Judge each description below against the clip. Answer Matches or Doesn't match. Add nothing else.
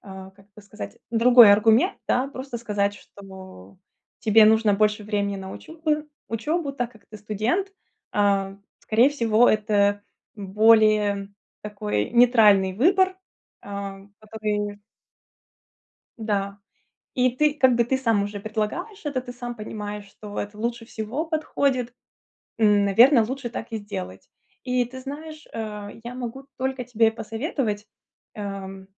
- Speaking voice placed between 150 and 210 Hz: Doesn't match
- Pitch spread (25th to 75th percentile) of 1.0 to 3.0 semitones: Doesn't match